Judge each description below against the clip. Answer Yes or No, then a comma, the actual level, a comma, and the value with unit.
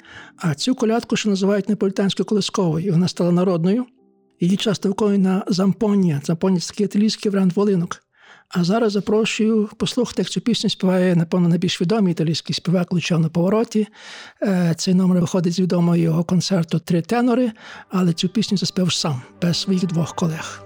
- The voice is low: No, medium, 185 Hz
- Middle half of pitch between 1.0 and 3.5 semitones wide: Yes, average, 3.1 semitones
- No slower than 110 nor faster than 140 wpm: No, average, 150 wpm